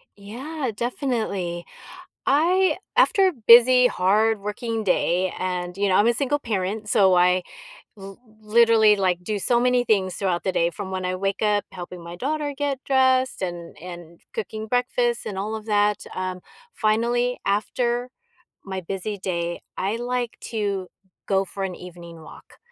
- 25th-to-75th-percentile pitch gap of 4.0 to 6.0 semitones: Yes, average, 4.5 semitones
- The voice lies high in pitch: Yes, high, 210 Hz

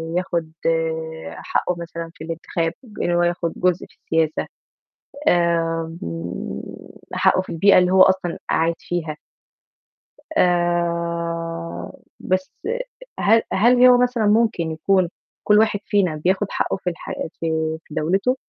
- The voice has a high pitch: No, medium, 175 Hz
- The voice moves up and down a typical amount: No, narrow, 2.3 semitones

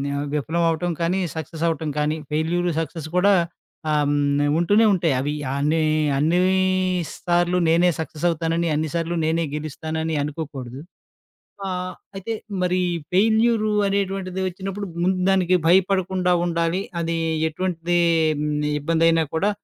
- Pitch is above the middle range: No, medium, 170 Hz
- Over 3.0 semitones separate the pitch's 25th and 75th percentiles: No, narrow, 2.6 semitones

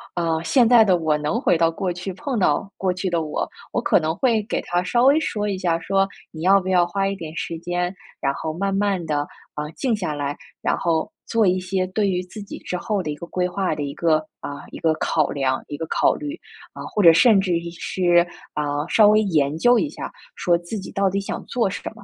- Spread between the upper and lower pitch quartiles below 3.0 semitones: No, average, 3.5 semitones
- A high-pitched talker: No, medium, 180 Hz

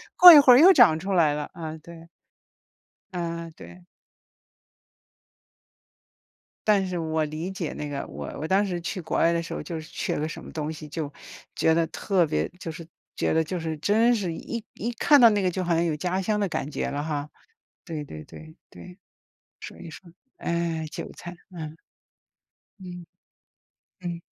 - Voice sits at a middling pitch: Yes, medium, 170 Hz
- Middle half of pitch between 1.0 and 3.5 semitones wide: Yes, average, 3.0 semitones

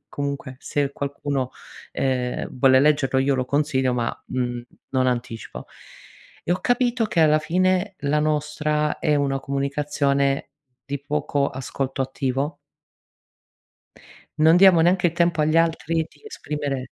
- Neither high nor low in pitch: Yes, medium, 145 Hz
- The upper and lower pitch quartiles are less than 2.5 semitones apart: No, average, 2.8 semitones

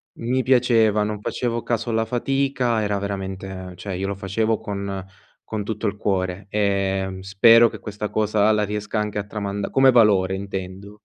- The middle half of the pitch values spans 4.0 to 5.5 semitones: No, narrow, 2.4 semitones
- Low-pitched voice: Yes, low, 105 Hz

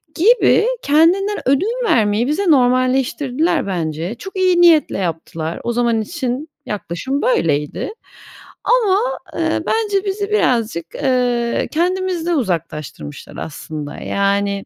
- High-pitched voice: Yes, very high, 255 Hz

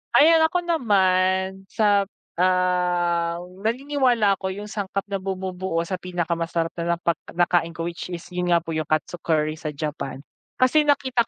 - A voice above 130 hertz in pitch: Yes, medium, 185 Hz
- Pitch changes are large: No, average, 3.2 semitones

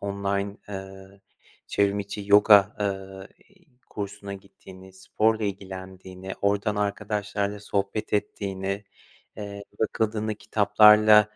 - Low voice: Yes, low, 100 Hz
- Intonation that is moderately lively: No, narrow, 1.3 semitones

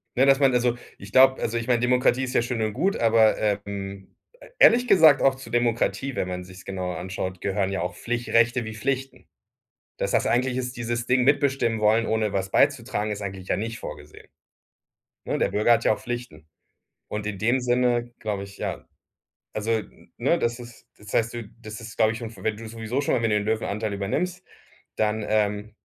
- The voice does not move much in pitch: No, average, 3.1 semitones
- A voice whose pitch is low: Yes, low, 115 Hz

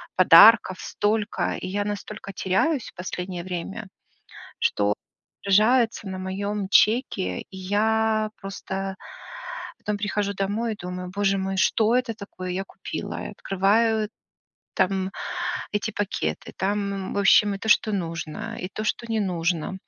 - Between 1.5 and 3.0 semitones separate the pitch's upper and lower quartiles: Yes, narrow, 2.4 semitones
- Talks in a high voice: Yes, high, 200 Hz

